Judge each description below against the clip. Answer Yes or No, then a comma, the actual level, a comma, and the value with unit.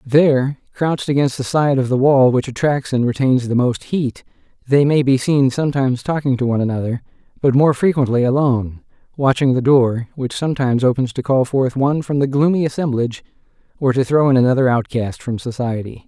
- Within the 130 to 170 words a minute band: No, average, 185 wpm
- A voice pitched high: No, low, 130 Hz